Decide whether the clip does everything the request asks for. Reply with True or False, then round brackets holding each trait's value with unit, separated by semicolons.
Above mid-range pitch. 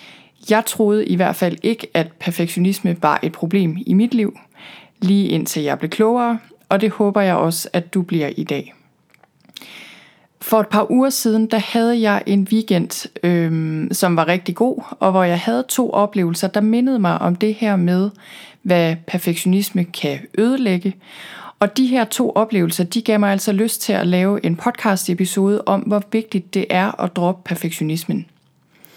True (200 Hz)